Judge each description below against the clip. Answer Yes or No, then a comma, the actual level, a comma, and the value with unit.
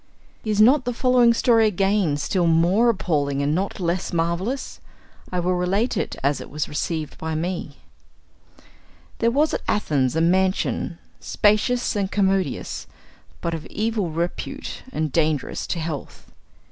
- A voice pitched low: No, medium, 180 Hz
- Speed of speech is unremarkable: Yes, average, 145 wpm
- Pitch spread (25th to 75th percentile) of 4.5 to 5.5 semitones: Yes, average, 5.0 semitones